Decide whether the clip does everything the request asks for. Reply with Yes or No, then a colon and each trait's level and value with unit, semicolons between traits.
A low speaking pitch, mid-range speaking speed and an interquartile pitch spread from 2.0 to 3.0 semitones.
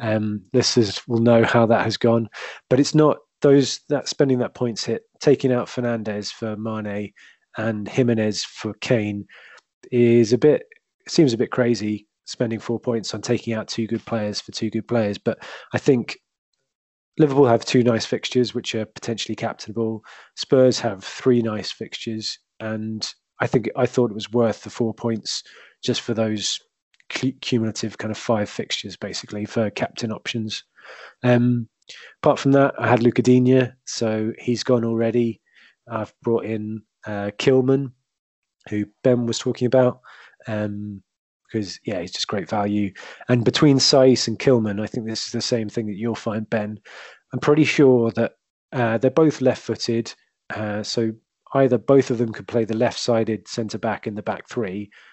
Yes: low, 115 Hz; average, 170 wpm; narrow, 2.4 semitones